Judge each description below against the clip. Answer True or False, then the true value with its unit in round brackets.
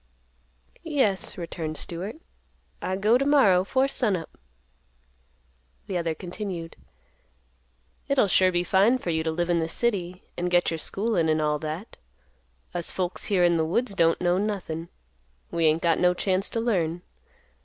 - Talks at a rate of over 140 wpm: True (160 wpm)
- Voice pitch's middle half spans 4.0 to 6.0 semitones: False (3.5 semitones)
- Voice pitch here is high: False (180 Hz)